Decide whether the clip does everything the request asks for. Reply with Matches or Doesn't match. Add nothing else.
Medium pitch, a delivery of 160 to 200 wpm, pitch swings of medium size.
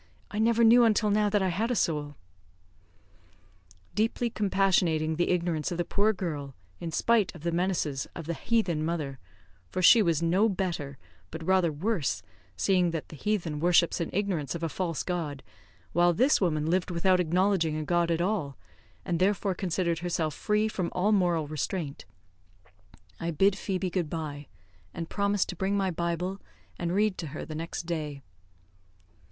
Matches